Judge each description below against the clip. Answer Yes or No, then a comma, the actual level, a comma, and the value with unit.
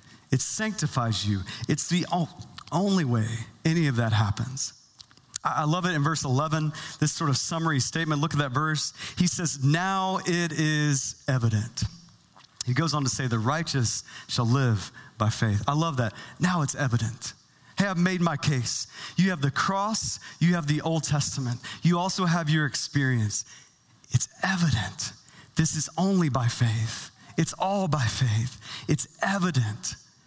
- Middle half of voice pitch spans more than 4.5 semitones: Yes, wide, 5.6 semitones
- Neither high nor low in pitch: Yes, medium, 145 Hz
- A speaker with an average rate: Yes, average, 160 wpm